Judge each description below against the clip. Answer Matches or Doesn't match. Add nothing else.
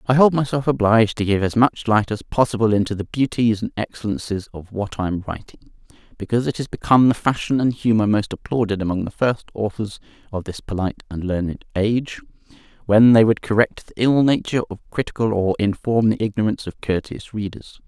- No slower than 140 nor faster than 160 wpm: Doesn't match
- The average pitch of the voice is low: Matches